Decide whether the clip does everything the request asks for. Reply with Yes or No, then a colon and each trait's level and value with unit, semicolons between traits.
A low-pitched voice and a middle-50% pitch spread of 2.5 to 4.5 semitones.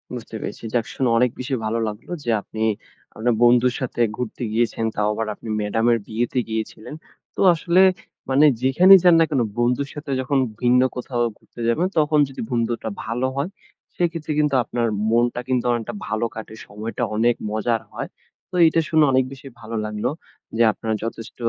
Yes: low, 120 Hz; average, 3.2 semitones